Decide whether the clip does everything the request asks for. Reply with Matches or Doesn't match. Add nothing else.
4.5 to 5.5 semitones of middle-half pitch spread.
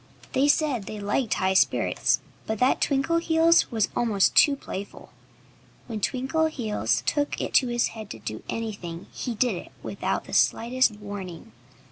Matches